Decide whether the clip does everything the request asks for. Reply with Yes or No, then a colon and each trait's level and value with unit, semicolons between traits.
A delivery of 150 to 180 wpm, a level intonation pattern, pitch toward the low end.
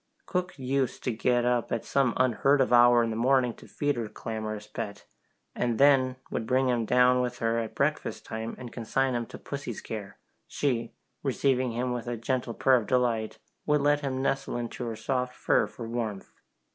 No: average, 195 wpm; narrow, 2.2 semitones; low, 125 Hz